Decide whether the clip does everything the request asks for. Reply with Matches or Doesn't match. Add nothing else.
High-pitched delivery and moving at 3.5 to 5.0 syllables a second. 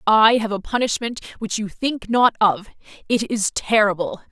Matches